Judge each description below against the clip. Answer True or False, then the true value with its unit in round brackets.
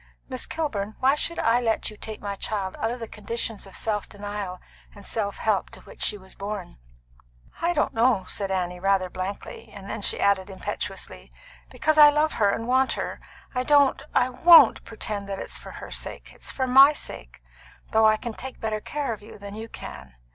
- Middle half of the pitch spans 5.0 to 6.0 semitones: False (4.1 semitones)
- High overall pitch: True (215 Hz)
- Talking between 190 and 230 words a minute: True (200 wpm)